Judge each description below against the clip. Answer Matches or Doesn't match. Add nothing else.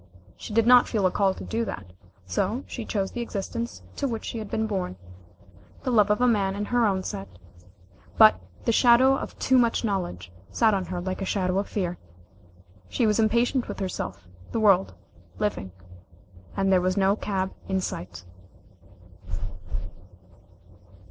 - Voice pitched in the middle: Doesn't match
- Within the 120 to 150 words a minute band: Doesn't match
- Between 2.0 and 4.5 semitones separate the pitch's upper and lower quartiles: Matches